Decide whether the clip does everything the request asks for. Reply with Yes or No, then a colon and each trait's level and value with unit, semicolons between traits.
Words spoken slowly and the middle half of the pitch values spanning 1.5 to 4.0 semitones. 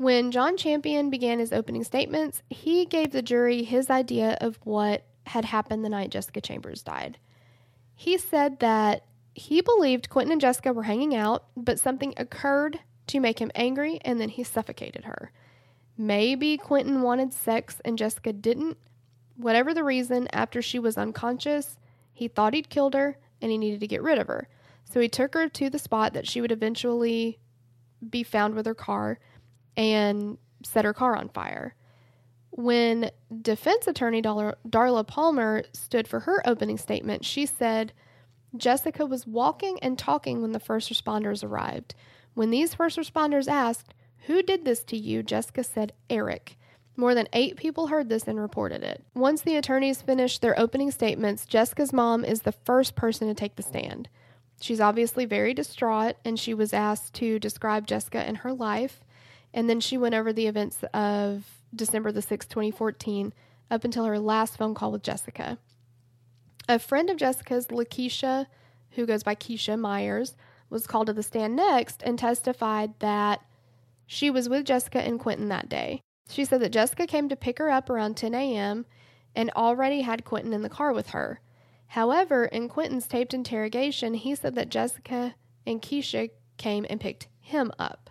No: average, 175 wpm; average, 3.7 semitones